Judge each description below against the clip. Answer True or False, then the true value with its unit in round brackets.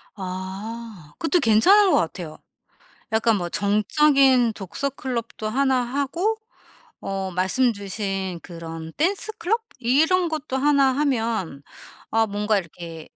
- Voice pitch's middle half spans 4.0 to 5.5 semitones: False (6.6 semitones)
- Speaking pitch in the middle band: False (225 Hz)